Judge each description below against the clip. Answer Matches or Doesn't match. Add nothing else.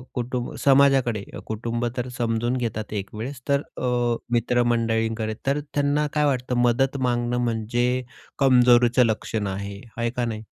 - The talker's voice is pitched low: Matches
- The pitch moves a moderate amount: Doesn't match